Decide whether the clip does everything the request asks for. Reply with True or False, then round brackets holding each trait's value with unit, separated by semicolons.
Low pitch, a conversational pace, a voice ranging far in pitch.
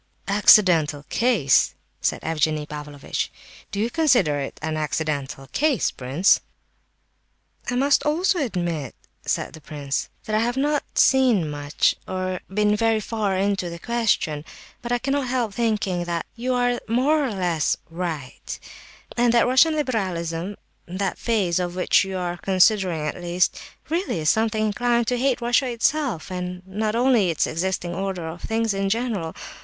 False (195 Hz; 150 wpm; 6.2 semitones)